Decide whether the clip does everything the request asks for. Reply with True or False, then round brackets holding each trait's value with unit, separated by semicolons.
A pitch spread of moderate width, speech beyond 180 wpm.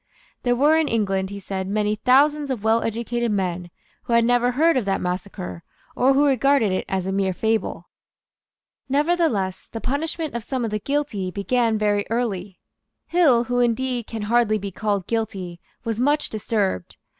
False (4.5 semitones; 170 wpm)